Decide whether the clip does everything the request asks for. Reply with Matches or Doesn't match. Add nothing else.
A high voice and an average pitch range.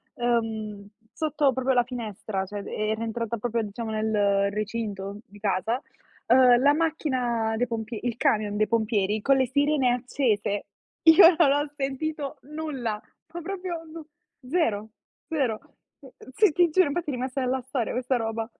Matches